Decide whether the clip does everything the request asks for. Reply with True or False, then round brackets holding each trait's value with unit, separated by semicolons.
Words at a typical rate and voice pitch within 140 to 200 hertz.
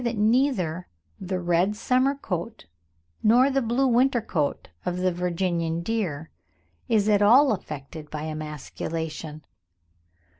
False (120 wpm; 185 Hz)